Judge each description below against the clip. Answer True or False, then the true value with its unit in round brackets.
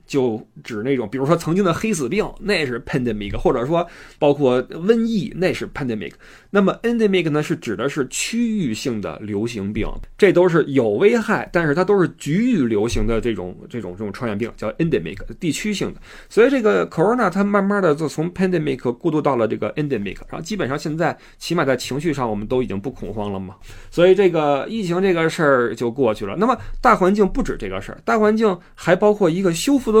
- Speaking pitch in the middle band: True (165 Hz)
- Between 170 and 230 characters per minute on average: False (390 characters per minute)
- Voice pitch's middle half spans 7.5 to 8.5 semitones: True (8.1 semitones)